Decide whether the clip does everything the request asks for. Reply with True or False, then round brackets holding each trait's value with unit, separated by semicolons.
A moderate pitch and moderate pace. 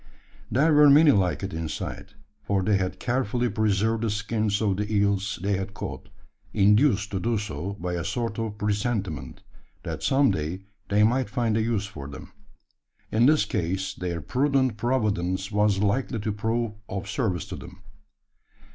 False (105 Hz; 165 wpm)